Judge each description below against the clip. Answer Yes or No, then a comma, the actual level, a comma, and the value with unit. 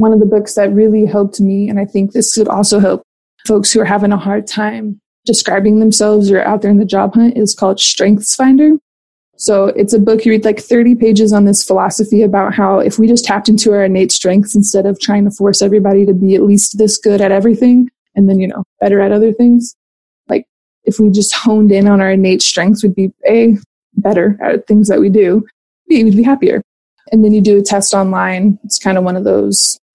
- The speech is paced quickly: Yes, fast, 230 wpm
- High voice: Yes, high, 205 Hz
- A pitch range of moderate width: No, narrow, 1.7 semitones